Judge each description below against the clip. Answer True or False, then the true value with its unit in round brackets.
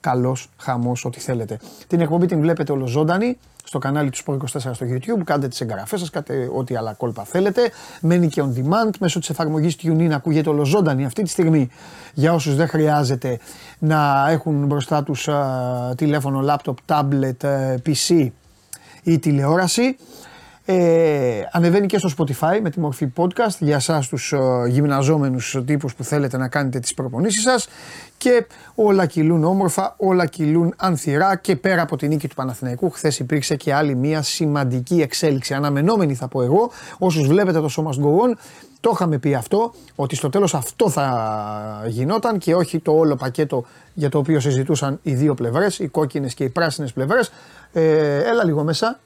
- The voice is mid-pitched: True (150 Hz)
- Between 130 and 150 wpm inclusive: False (165 wpm)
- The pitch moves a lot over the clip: False (3.9 semitones)